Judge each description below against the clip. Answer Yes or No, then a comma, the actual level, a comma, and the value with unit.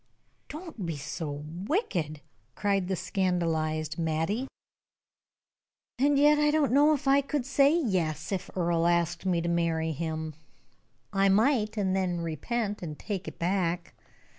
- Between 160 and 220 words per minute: No, average, 140 wpm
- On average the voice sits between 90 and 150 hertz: No, medium, 185 Hz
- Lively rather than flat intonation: Yes, wide, 7.0 semitones